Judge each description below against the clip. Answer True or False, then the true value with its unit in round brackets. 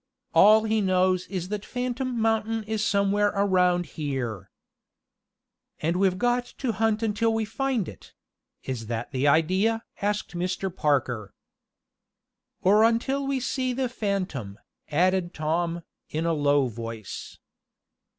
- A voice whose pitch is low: False (190 Hz)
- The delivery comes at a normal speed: False (130 wpm)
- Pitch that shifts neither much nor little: False (6.1 semitones)